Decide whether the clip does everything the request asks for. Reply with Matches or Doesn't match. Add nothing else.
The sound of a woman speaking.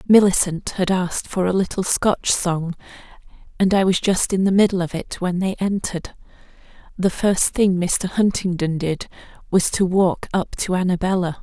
Matches